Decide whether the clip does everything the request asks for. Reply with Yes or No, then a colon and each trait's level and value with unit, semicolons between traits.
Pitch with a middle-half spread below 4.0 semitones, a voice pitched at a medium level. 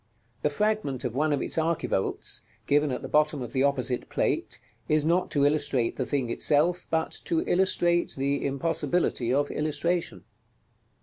Yes: average, 3.2 semitones; medium, 145 Hz